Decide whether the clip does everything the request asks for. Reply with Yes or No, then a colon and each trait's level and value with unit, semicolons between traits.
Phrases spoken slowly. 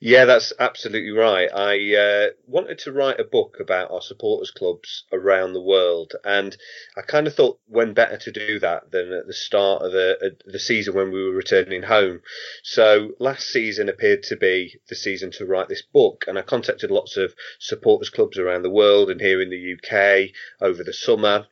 No: average, 200 wpm